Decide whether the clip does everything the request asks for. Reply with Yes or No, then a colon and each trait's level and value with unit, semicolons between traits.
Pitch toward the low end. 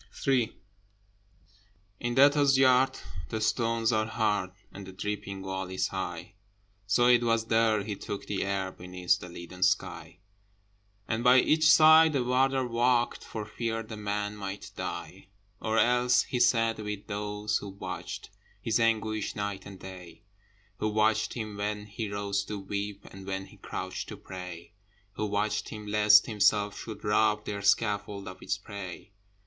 Yes: low, 105 Hz